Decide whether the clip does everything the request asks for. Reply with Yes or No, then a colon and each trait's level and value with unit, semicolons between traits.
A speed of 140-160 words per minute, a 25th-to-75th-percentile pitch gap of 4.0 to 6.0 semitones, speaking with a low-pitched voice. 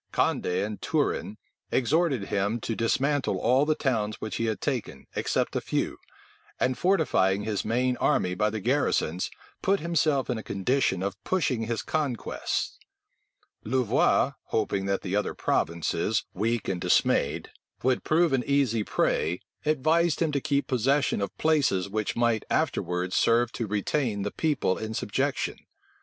Yes: average, 150 wpm; wide, 5.4 semitones; low, 115 Hz